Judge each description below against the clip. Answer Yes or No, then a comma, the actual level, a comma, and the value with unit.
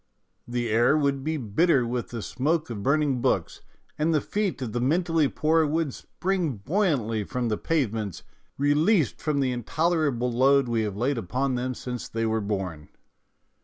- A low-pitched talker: Yes, low, 130 Hz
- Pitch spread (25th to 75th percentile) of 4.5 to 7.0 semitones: Yes, average, 5.0 semitones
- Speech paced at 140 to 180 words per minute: Yes, average, 170 wpm